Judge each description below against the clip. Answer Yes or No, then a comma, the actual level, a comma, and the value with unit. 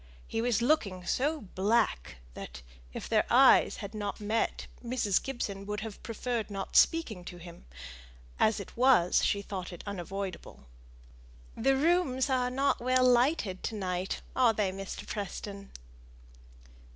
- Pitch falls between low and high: No, high, 215 Hz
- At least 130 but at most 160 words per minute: Yes, average, 140 wpm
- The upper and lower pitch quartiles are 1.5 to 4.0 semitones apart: No, average, 4.5 semitones